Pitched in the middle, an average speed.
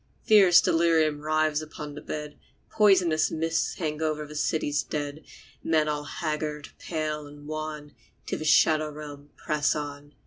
Yes: medium, 155 Hz; average, 145 wpm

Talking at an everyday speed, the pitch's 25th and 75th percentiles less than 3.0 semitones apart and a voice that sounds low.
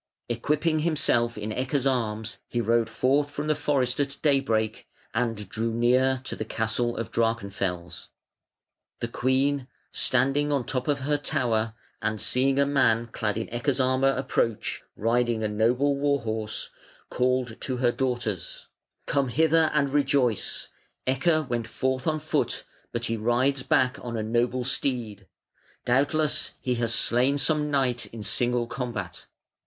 No: average, 150 wpm; average, 3.3 semitones; low, 125 Hz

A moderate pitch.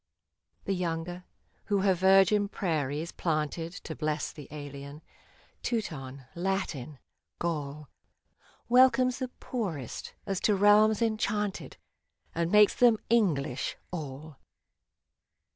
Yes: medium, 175 Hz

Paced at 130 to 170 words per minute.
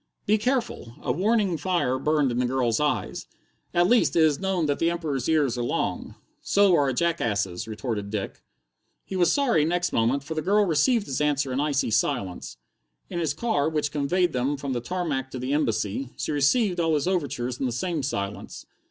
No: average, 195 wpm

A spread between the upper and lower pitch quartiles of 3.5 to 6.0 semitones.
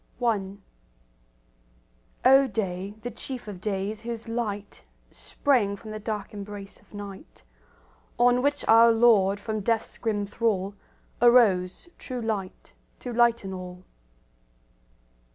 No: average, 3.1 semitones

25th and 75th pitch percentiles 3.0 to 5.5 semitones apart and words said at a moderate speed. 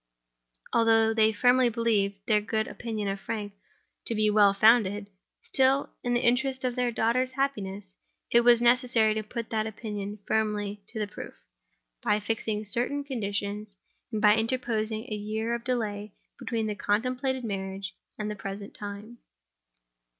No: narrow, 2.5 semitones; average, 150 wpm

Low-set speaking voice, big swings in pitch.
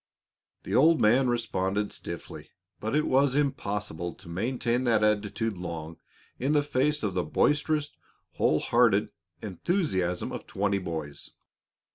Yes: low, 105 Hz; wide, 6.3 semitones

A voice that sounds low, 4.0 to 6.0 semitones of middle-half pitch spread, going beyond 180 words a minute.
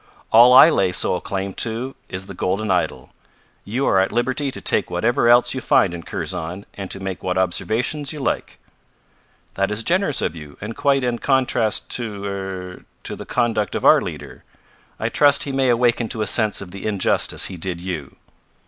Yes: low, 110 Hz; average, 4.7 semitones; average, 195 wpm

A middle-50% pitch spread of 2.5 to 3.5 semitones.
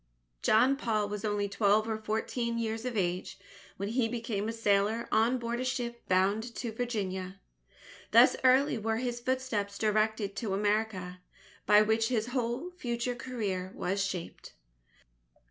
Yes: average, 2.8 semitones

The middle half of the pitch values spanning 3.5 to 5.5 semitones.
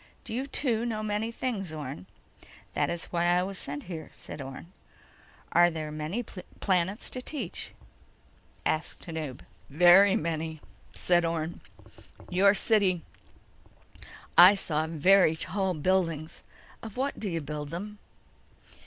Yes: average, 4.2 semitones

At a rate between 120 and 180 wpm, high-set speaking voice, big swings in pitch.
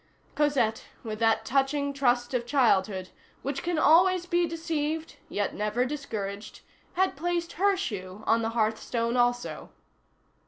Yes: average, 140 wpm; very high, 255 Hz; wide, 6.2 semitones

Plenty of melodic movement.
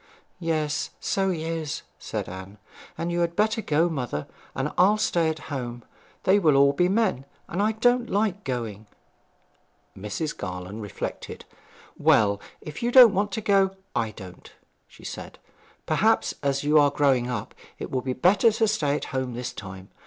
Yes: wide, 8.0 semitones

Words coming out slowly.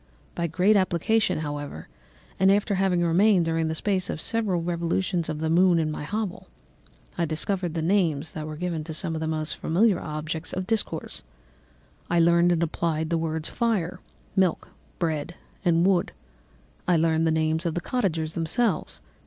No: average, 175 wpm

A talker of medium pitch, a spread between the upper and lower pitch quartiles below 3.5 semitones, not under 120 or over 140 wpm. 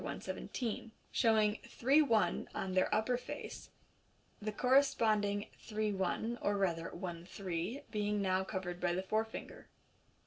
No: high, 210 Hz; average, 3.1 semitones; slow, 135 wpm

